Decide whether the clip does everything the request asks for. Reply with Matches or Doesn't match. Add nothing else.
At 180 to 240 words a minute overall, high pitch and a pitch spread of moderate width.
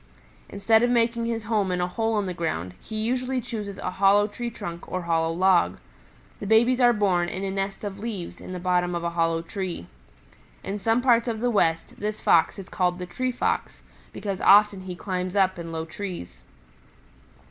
Matches